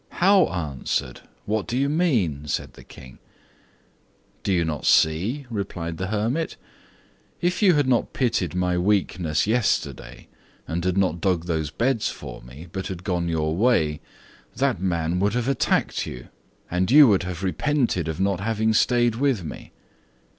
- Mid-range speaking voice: No, very low, 95 Hz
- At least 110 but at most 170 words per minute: Yes, average, 160 wpm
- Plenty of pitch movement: Yes, wide, 6.3 semitones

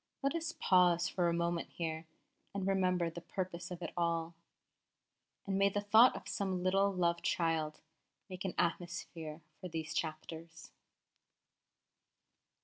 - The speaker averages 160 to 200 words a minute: No, average, 140 wpm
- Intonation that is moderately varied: No, narrow, 2.3 semitones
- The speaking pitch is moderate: Yes, medium, 175 Hz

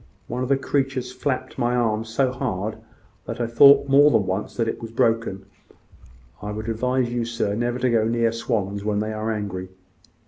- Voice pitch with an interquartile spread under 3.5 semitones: Yes, average, 2.8 semitones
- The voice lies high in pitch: No, low, 115 Hz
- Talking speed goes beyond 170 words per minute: Yes, average, 185 wpm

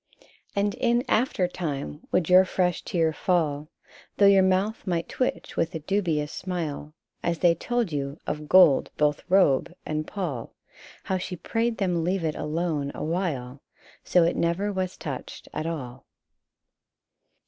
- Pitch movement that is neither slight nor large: Yes, average, 3.8 semitones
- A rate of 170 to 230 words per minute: No, average, 150 wpm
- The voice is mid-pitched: Yes, medium, 170 Hz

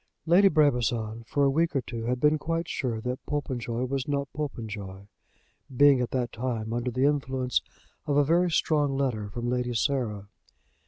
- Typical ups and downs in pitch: Yes, average, 3.5 semitones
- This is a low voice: Yes, low, 130 Hz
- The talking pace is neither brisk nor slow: Yes, average, 170 wpm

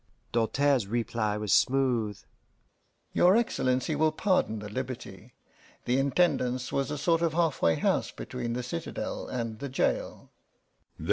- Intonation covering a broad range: No, average, 4.2 semitones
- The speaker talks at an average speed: No, slow, 130 wpm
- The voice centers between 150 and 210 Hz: No, low, 125 Hz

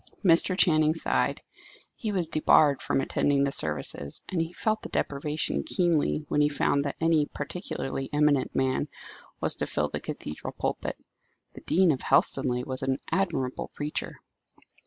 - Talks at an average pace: Yes, average, 155 wpm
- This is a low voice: No, medium, 150 Hz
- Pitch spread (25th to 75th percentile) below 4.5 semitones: Yes, average, 3.5 semitones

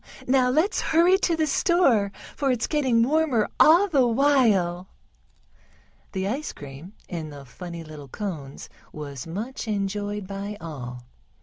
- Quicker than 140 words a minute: No, slow, 135 wpm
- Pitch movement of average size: No, wide, 8.6 semitones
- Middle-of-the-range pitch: No, high, 210 Hz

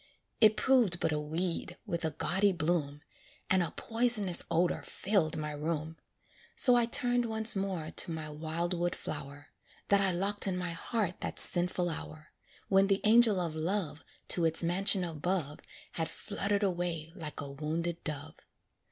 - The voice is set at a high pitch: No, medium, 175 Hz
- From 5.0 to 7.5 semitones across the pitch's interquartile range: No, average, 3.8 semitones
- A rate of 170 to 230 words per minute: No, average, 160 wpm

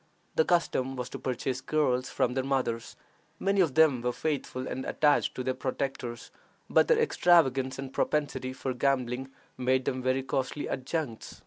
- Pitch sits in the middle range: No, low, 130 Hz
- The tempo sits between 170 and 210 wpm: No, average, 160 wpm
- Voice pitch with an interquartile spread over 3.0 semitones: No, narrow, 2.4 semitones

